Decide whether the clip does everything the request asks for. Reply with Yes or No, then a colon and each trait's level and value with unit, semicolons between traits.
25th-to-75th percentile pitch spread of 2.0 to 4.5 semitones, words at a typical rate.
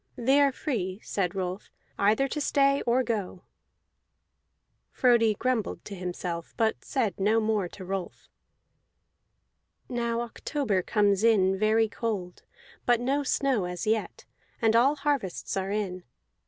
No: average, 4.2 semitones; slow, 130 wpm